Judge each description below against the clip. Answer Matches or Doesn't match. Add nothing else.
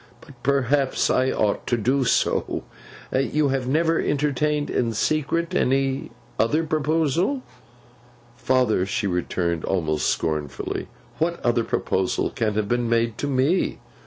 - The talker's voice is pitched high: Doesn't match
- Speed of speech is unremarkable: Doesn't match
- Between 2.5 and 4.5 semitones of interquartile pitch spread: Doesn't match